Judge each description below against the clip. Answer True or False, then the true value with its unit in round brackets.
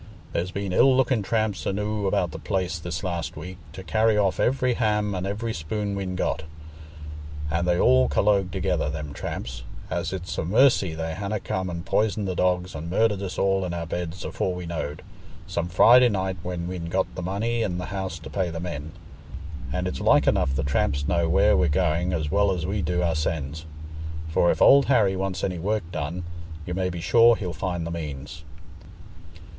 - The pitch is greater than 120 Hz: False (90 Hz)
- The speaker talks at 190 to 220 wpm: True (195 wpm)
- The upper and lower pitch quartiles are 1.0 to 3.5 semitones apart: True (3.2 semitones)